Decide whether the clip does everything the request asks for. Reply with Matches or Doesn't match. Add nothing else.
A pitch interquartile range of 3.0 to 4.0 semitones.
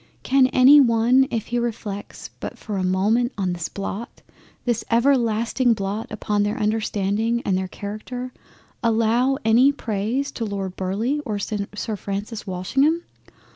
Matches